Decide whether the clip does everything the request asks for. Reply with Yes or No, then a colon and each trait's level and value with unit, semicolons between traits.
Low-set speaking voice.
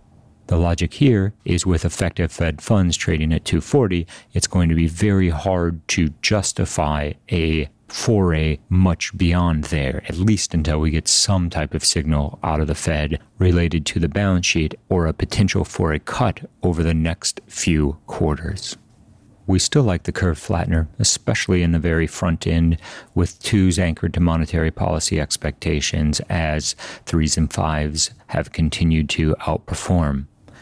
Yes: very low, 85 Hz